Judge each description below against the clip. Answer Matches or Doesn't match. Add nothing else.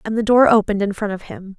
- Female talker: Matches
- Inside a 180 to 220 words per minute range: Doesn't match